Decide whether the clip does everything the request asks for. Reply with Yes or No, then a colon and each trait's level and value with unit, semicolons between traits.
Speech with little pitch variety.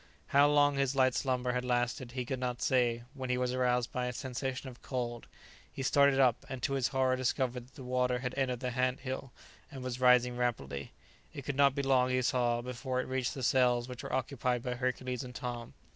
Yes: narrow, 1.1 semitones